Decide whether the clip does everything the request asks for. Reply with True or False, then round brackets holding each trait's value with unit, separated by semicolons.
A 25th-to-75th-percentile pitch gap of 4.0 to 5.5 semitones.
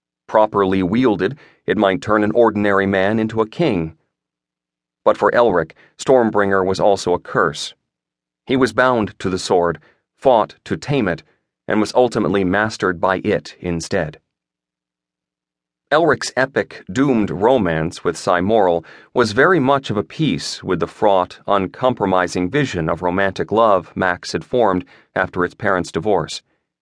True (4.6 semitones)